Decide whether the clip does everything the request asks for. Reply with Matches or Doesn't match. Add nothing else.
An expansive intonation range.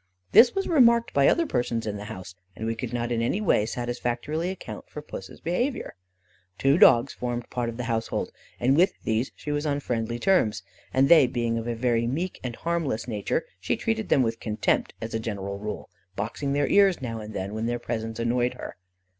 Doesn't match